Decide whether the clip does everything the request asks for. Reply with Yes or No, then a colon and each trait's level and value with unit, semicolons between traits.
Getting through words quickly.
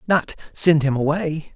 No: slow, 115 wpm